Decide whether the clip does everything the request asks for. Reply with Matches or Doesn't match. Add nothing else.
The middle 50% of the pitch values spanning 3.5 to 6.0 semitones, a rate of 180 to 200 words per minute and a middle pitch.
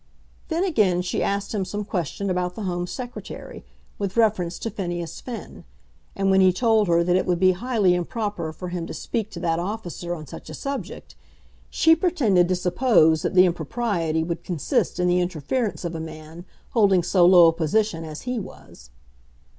Matches